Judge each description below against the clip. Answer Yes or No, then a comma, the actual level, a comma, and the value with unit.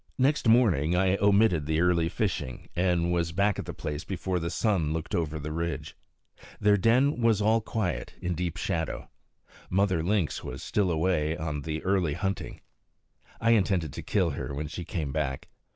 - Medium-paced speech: Yes, average, 175 wpm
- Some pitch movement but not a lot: Yes, average, 4.2 semitones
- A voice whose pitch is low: Yes, very low, 90 Hz